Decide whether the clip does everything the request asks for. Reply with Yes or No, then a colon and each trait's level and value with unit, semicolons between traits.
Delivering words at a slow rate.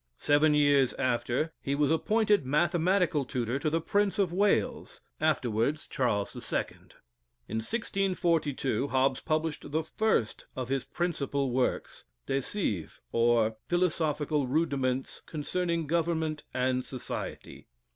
Yes: slow, 115 wpm